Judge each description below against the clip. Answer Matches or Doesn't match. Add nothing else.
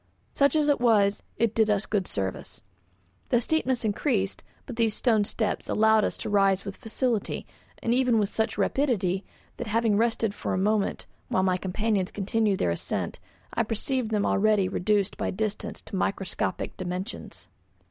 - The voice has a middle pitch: Doesn't match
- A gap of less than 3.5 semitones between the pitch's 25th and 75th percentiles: Matches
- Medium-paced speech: Matches